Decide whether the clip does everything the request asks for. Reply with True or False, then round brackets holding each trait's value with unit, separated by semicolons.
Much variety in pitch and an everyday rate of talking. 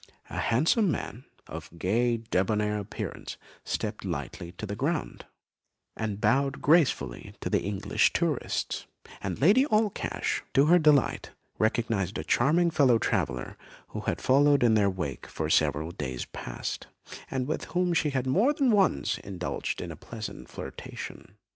True (7.7 semitones; 150 wpm)